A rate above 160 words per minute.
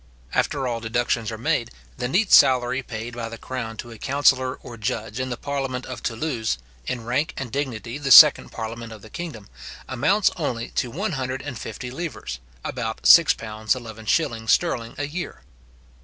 No: average, 155 wpm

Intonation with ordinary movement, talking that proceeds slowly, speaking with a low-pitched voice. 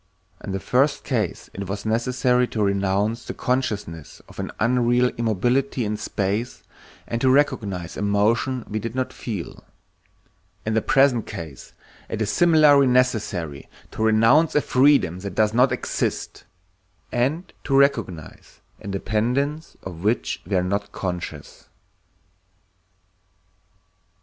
Yes: average, 4.3 semitones; slow, 130 wpm; low, 115 Hz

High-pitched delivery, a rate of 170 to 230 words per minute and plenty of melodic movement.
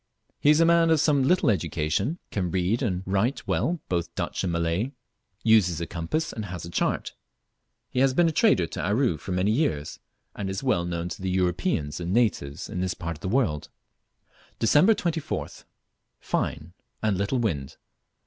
No: very low, 95 Hz; average, 180 wpm; wide, 7.7 semitones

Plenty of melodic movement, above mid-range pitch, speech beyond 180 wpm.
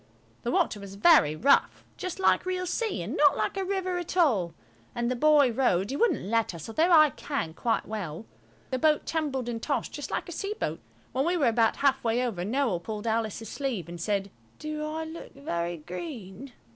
Yes: wide, 7.3 semitones; very high, 255 Hz; fast, 205 wpm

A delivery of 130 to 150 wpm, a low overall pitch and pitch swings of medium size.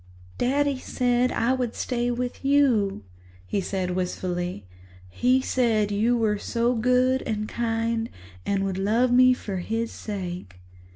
No: average, 140 wpm; high, 230 Hz; average, 4.1 semitones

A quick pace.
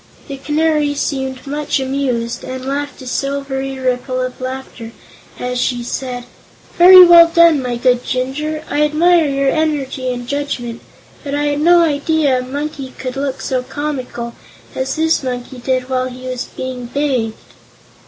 No: average, 155 wpm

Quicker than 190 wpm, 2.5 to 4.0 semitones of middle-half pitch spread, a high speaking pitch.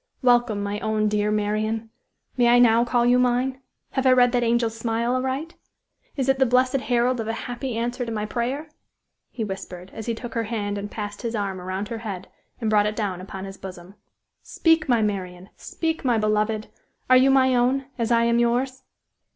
Yes: average, 200 wpm; average, 3.0 semitones; high, 230 Hz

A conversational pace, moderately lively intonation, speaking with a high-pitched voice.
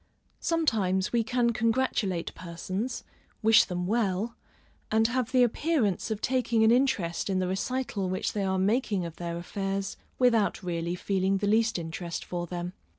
Yes: average, 155 wpm; average, 4.4 semitones; high, 200 Hz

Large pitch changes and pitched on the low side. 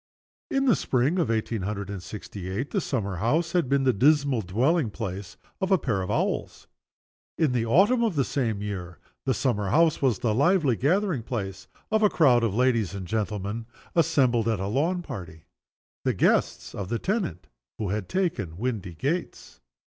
Yes: wide, 7.5 semitones; low, 120 Hz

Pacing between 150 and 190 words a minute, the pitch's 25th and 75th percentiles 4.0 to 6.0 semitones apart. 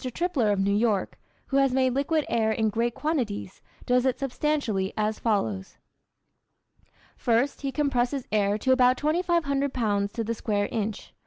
Yes: average, 155 wpm; average, 4.6 semitones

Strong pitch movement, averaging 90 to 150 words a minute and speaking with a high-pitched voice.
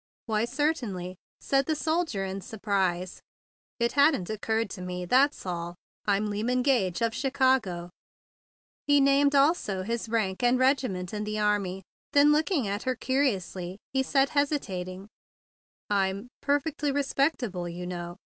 Yes: wide, 6.6 semitones; slow, 135 wpm; high, 225 Hz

